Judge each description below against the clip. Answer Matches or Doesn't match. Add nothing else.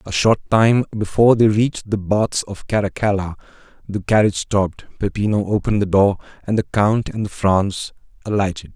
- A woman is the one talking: Doesn't match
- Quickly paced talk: Doesn't match